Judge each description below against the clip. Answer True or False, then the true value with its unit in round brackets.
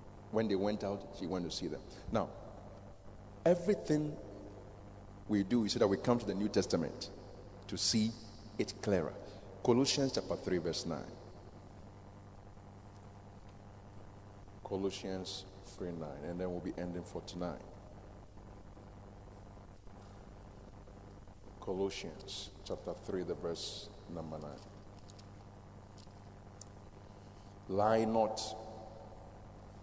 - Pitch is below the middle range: True (100 Hz)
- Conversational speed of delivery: False (100 wpm)